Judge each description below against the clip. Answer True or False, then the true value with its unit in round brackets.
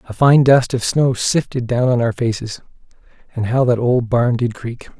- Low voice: True (125 Hz)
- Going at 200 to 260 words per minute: True (205 wpm)